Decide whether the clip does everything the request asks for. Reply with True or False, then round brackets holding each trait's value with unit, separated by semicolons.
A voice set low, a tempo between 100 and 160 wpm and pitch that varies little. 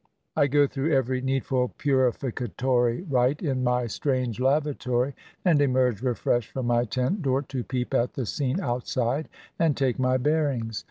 True (130 Hz; 155 wpm; 2.2 semitones)